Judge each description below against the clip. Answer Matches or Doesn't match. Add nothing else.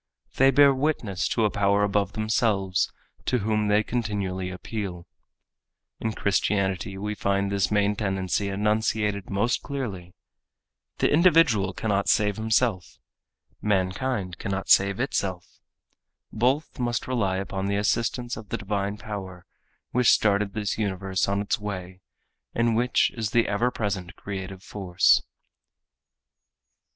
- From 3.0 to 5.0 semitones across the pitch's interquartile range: Doesn't match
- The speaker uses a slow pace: Matches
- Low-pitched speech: Matches